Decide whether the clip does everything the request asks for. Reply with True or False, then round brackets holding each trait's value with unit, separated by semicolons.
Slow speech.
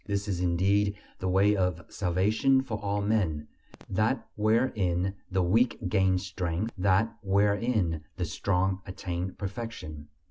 True (130 wpm)